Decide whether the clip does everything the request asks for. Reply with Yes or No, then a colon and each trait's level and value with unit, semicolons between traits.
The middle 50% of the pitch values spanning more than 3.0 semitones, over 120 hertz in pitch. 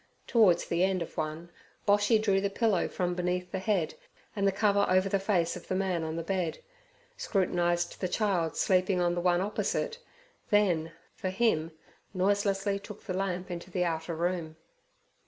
No: narrow, 2.5 semitones; medium, 185 Hz